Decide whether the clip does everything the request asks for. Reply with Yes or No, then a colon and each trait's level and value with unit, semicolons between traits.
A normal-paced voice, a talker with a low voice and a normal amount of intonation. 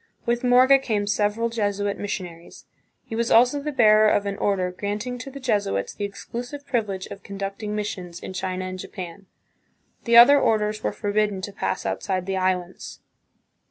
No: average, 170 wpm; high, 205 Hz; average, 3.6 semitones